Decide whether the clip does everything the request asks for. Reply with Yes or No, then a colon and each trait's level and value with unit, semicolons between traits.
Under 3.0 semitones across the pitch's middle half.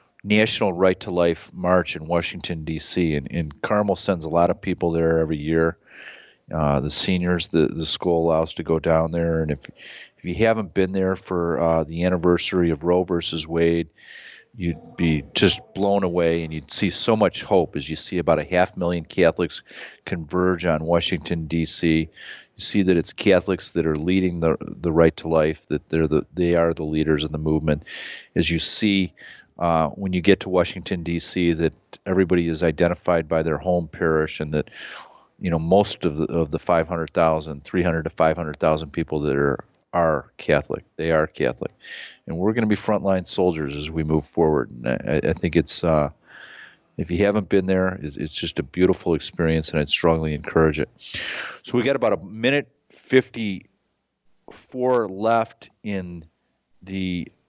Yes: narrow, 2.4 semitones